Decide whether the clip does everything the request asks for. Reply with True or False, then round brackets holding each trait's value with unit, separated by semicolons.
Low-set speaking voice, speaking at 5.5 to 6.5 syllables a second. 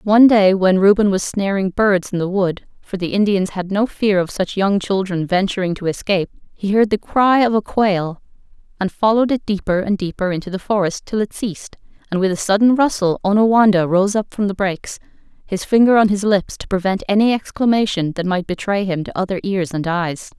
False (195 Hz; 5.6 syllables/s)